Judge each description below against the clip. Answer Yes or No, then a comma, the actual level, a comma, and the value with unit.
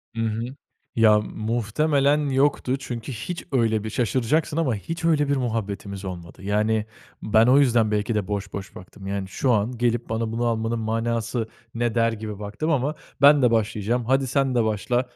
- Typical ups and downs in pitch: Yes, average, 3.2 semitones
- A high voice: No, low, 115 Hz